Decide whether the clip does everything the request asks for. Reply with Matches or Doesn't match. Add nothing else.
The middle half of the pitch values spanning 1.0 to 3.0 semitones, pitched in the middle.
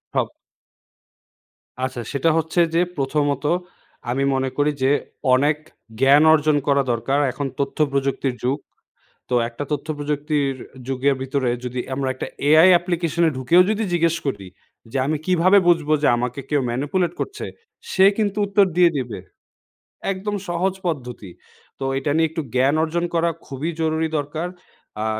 Doesn't match